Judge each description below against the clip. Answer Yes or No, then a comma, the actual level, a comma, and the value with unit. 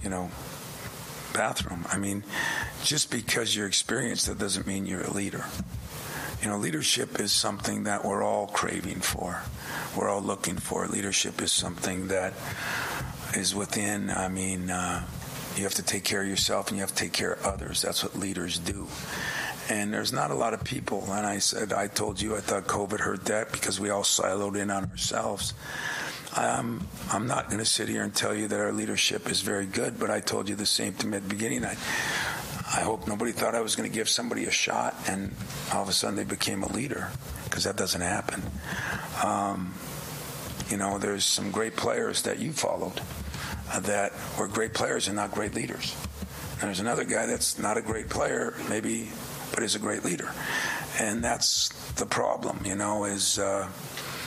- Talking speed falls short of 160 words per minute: No, average, 195 wpm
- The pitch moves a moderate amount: No, narrow, 1.4 semitones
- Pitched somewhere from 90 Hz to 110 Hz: Yes, low, 100 Hz